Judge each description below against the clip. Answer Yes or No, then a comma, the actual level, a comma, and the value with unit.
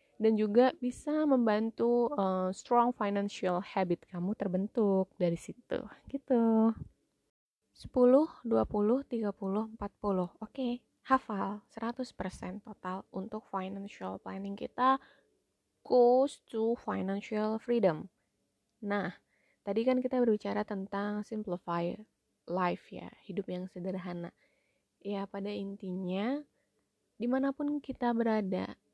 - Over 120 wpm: No, average, 100 wpm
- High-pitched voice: Yes, high, 210 Hz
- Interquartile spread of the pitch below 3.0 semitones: No, average, 3.9 semitones